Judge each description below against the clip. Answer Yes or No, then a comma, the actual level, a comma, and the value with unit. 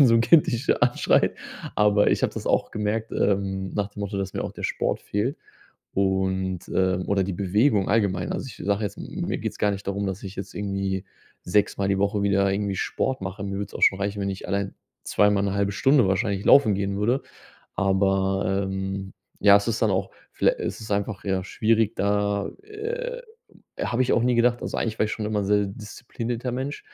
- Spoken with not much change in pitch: Yes, narrow, 2.3 semitones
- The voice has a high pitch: No, low, 100 Hz